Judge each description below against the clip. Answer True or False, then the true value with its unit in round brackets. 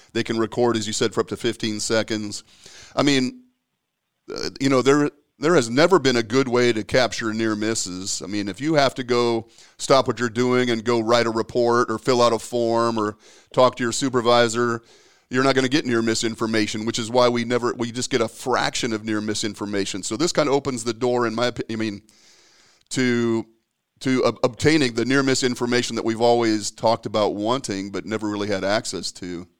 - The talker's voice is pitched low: True (115 Hz)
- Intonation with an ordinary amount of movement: False (2.2 semitones)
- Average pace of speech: False (210 wpm)